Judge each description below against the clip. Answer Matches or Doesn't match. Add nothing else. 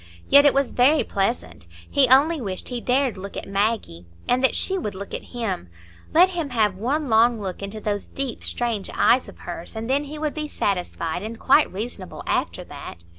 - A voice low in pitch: Doesn't match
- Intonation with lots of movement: Matches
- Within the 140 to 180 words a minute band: Doesn't match